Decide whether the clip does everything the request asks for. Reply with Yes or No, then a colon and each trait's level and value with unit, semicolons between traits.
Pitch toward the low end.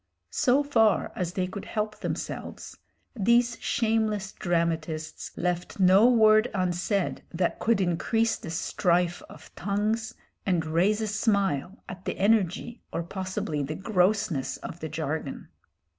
No: high, 195 Hz